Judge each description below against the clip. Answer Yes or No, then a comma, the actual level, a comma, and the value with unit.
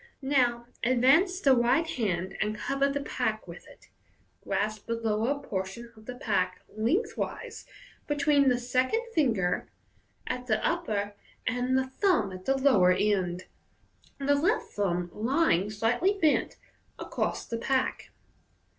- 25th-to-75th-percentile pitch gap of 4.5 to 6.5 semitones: Yes, average, 5.0 semitones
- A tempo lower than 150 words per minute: Yes, slow, 135 wpm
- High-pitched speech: Yes, high, 245 Hz